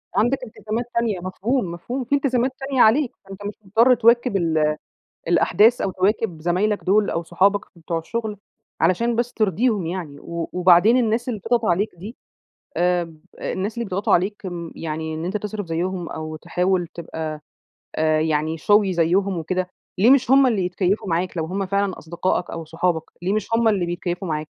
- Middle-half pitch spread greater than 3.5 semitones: Yes, average, 4.4 semitones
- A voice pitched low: No, high, 190 Hz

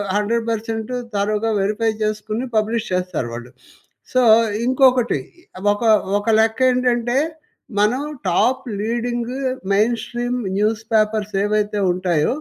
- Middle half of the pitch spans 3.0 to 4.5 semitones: No, narrow, 2.5 semitones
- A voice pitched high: Yes, high, 220 Hz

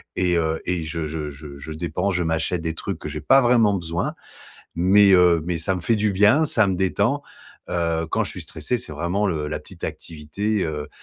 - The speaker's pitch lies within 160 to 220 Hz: No, very low, 85 Hz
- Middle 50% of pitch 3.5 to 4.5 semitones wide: Yes, average, 4.0 semitones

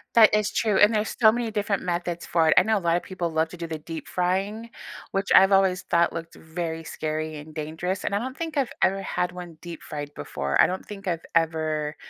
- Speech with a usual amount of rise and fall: Yes, average, 3.9 semitones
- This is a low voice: No, medium, 175 Hz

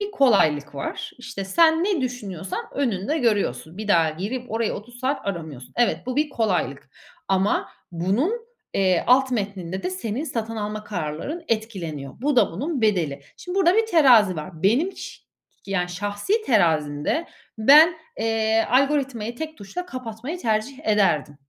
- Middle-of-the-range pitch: No, high, 220 Hz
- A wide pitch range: Yes, wide, 6.8 semitones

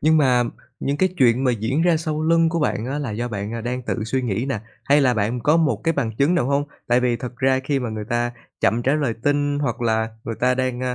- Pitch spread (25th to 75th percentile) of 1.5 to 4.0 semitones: Yes, average, 3.6 semitones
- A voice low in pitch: Yes, low, 125 Hz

